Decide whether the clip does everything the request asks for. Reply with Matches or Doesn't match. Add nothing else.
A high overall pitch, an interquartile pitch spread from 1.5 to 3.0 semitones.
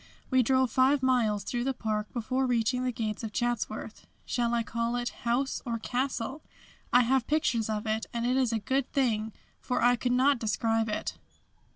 Matches